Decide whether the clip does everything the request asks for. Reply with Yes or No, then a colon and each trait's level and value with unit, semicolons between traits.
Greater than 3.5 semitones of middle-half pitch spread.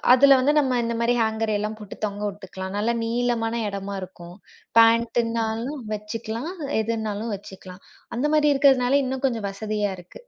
No: average, 3.0 semitones